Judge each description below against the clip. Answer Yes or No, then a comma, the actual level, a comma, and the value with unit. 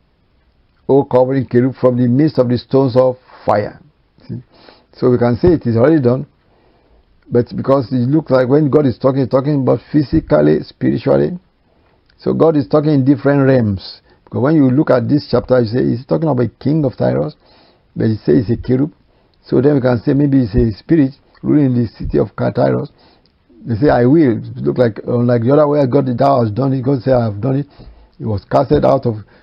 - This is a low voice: Yes, low, 130 Hz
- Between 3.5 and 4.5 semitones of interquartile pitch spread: No, average, 2.8 semitones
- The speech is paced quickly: Yes, fast, 210 wpm